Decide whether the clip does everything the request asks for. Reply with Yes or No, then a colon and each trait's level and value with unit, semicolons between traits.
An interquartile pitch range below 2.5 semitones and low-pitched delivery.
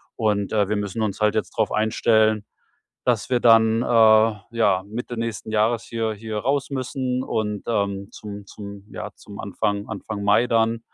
Yes: narrow, 2.0 semitones; low, 110 Hz